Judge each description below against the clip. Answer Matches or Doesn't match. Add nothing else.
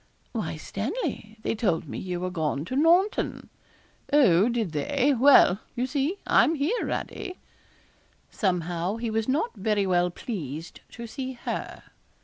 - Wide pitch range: Matches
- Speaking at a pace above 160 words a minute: Doesn't match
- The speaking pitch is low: Doesn't match